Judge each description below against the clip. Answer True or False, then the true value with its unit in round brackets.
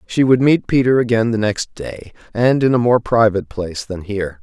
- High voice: False (115 Hz)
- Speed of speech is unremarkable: False (215 wpm)